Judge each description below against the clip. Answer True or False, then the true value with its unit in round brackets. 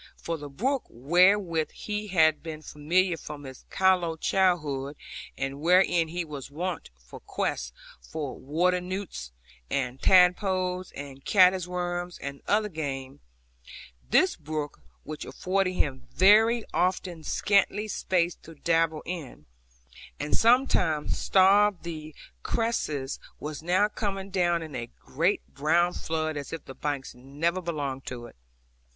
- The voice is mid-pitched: True (170 Hz)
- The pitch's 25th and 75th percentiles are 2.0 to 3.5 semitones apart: False (4.2 semitones)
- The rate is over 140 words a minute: False (135 wpm)